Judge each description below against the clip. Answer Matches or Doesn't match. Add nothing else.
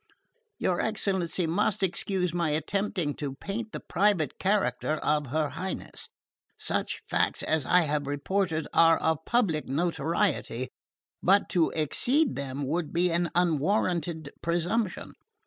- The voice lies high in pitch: Doesn't match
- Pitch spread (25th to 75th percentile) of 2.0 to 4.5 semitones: Matches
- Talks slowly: Matches